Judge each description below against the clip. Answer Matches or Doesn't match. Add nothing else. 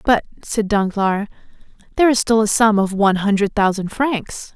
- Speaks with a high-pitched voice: Matches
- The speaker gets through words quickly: Doesn't match